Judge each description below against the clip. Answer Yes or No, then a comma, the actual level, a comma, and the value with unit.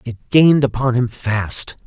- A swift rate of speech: No, average, 160 wpm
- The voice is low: Yes, low, 125 Hz